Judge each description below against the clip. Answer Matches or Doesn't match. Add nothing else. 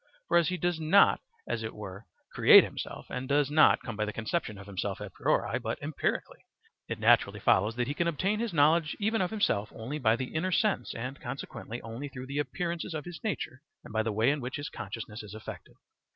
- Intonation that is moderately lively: Doesn't match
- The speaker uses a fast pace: Matches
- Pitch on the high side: Doesn't match